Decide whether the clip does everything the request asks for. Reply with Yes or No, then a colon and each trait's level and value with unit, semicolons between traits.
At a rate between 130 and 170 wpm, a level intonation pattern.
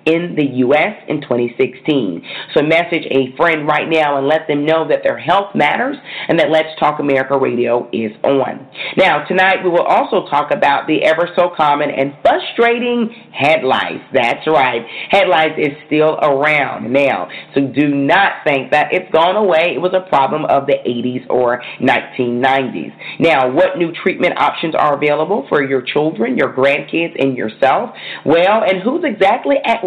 No: average, 165 wpm; average, 4.2 semitones